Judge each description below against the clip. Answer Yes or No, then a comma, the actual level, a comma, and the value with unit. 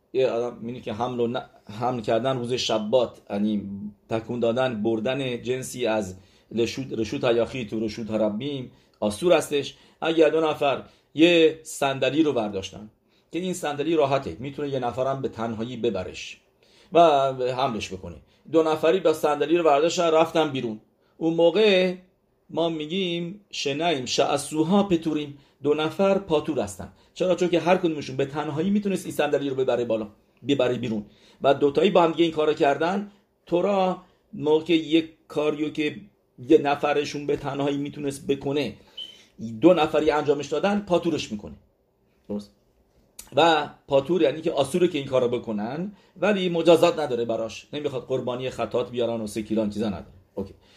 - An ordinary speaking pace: Yes, average, 145 wpm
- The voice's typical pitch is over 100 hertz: Yes, medium, 140 Hz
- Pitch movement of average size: No, wide, 5.8 semitones